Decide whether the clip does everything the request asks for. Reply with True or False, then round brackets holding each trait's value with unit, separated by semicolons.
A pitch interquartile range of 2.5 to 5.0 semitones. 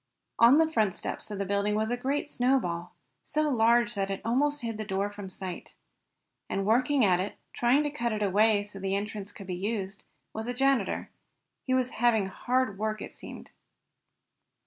True (3.9 semitones)